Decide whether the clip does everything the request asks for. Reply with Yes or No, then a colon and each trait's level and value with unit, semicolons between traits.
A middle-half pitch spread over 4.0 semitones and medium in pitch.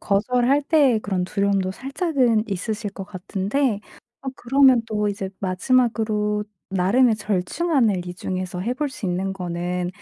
No: average, 5.1 semitones; high, 210 Hz